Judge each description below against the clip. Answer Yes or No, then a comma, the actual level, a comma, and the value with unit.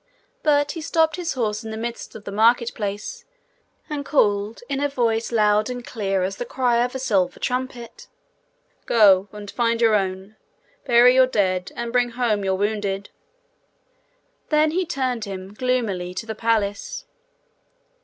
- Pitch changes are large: No, average, 3.7 semitones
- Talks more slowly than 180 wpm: Yes, average, 160 wpm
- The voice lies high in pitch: Yes, high, 230 Hz